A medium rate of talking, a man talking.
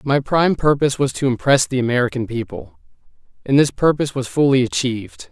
Yes: average, 170 wpm; male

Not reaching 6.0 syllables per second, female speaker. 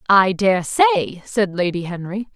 Yes: 4.6 syllables/s; female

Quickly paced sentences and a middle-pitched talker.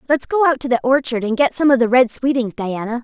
No: fast, 275 wpm; very high, 255 Hz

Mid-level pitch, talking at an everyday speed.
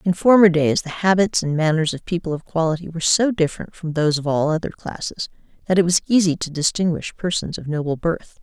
No: medium, 165 Hz; fast, 215 wpm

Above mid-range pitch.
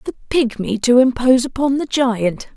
Yes: high, 245 Hz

